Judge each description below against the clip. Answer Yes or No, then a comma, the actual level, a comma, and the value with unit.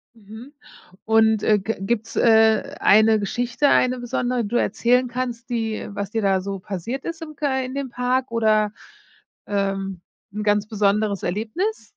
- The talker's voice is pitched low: No, high, 225 Hz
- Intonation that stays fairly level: No, average, 3.3 semitones